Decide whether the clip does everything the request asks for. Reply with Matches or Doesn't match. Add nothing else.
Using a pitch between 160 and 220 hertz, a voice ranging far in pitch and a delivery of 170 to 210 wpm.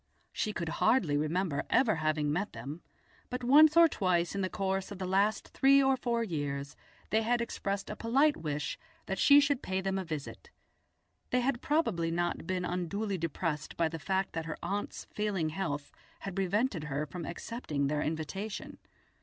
Matches